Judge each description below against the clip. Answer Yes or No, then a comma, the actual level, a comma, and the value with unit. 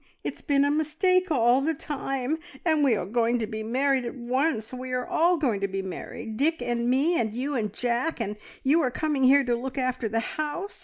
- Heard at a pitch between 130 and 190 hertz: No, very high, 260 Hz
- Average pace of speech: No, fast, 220 wpm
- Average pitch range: Yes, average, 4.0 semitones